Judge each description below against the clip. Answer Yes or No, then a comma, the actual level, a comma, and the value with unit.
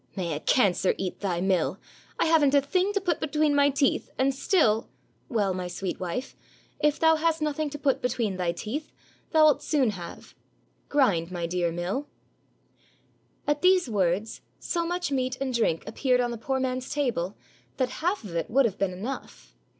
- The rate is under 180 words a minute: No, average, 190 wpm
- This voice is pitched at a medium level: No, very high, 255 Hz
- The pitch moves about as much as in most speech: No, wide, 7.5 semitones